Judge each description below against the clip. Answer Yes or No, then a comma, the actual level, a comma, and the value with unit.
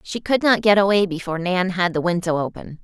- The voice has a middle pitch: Yes, medium, 180 Hz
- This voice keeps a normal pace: No, fast, 235 wpm